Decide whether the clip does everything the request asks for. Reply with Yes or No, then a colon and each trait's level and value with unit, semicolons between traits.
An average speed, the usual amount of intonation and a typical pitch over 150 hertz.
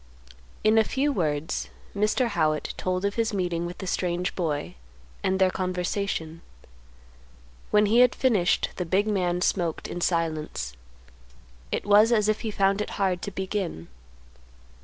Yes: average, 150 wpm; average, 3.4 semitones; medium, 185 Hz